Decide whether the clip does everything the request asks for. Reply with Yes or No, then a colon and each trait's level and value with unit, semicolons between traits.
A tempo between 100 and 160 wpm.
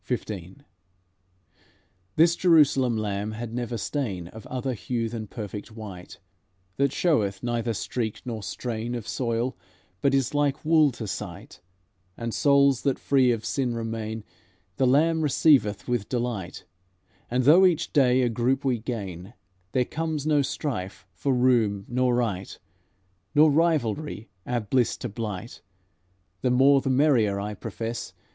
Yes: average, 140 wpm